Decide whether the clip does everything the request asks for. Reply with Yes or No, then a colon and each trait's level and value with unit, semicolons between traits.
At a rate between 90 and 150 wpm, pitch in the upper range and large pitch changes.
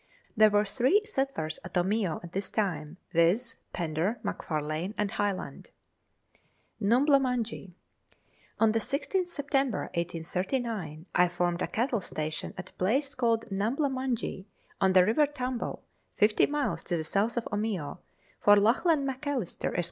Yes: average, 140 wpm; high, 210 Hz; wide, 6.4 semitones